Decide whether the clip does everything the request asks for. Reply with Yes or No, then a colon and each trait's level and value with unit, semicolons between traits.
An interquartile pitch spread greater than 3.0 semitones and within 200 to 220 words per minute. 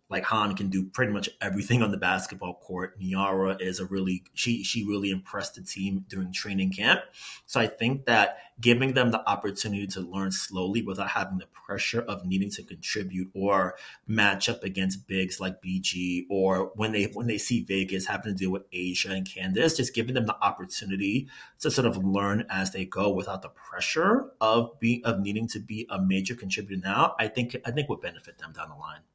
No: average, 2.7 semitones; fast, 205 wpm